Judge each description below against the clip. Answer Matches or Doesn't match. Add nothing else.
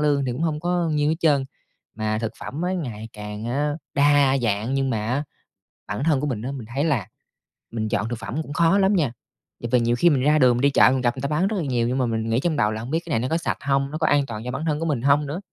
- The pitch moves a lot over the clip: Doesn't match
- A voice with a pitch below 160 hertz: Matches